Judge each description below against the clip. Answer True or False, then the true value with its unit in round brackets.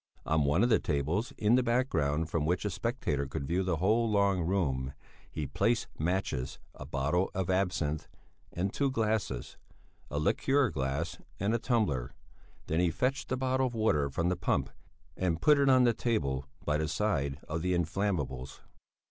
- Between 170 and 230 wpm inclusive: True (175 wpm)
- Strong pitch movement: True (7.1 semitones)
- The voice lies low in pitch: True (90 Hz)